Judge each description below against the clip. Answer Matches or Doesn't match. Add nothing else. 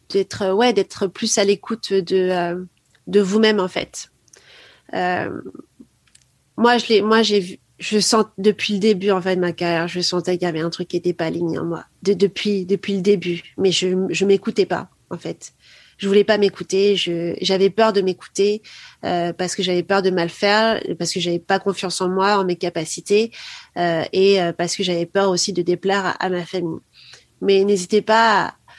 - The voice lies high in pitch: Matches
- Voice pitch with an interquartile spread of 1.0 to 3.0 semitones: Matches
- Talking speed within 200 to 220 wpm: Matches